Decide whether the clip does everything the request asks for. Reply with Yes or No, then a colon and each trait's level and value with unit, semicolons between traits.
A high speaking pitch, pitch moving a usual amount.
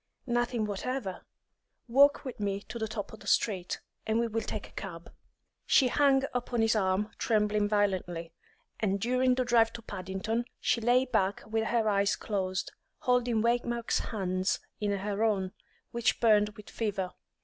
Yes: high, 220 Hz; average, 3.1 semitones